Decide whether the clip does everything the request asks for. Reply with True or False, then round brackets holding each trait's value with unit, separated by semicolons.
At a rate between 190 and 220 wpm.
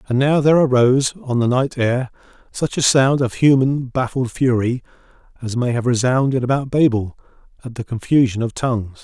False (175 wpm)